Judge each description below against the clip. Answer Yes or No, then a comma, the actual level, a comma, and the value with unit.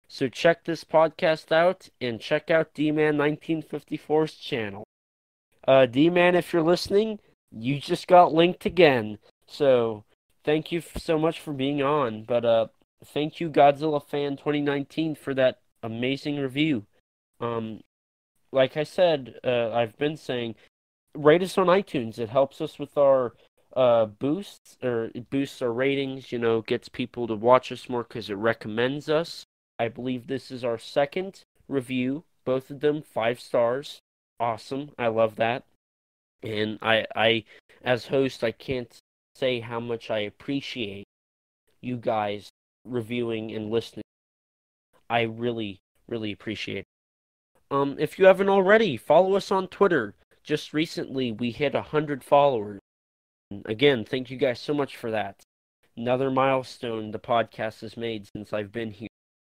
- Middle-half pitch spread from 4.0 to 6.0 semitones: Yes, average, 5.0 semitones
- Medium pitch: No, low, 130 Hz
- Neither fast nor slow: Yes, average, 150 wpm